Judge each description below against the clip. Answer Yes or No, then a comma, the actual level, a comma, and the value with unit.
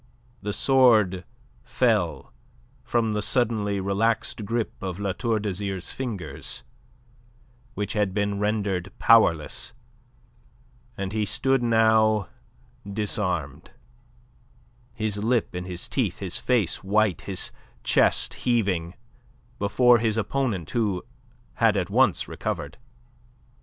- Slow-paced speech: Yes, slow, 105 wpm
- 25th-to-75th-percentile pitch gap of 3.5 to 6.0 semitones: No, average, 2.9 semitones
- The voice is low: Yes, low, 105 Hz